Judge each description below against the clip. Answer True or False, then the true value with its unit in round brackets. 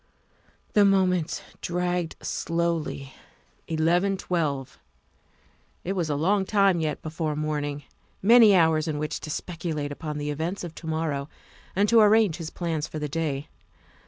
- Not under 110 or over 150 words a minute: True (145 wpm)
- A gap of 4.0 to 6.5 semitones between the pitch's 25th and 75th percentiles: False (3.1 semitones)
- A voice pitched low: False (165 Hz)